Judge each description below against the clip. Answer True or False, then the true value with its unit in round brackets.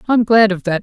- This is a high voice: True (205 Hz)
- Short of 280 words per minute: False (290 wpm)